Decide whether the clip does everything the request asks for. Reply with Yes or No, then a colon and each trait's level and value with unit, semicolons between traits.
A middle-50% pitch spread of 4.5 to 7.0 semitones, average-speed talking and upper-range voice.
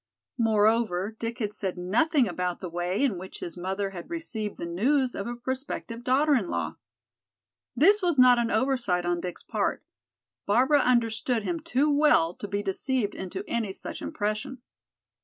Yes: average, 5.3 semitones; average, 165 wpm; high, 225 Hz